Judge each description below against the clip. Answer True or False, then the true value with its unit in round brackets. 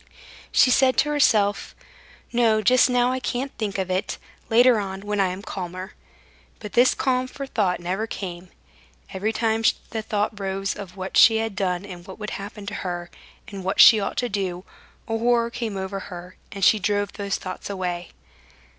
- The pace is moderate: True (185 wpm)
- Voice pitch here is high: True (205 Hz)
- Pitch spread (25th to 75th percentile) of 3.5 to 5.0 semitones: False (3.1 semitones)